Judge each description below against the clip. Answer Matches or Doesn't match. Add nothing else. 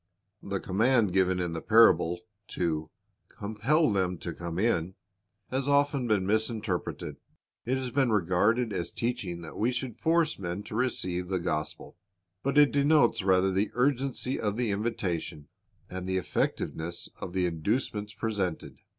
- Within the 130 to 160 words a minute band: Matches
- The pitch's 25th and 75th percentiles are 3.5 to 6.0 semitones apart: Matches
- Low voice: Matches